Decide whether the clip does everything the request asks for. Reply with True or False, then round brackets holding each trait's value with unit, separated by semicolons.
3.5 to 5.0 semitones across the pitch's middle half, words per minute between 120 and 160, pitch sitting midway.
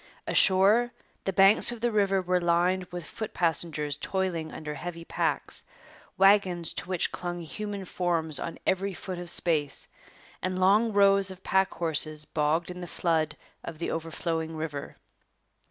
False (2.9 semitones; 155 wpm; 175 Hz)